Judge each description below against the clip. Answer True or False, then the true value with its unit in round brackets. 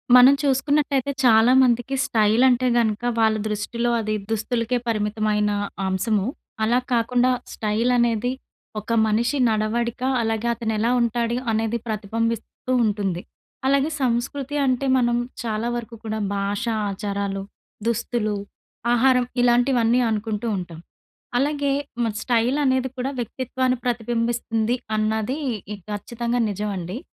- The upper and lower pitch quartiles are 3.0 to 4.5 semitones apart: False (2.5 semitones)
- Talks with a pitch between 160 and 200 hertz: False (230 Hz)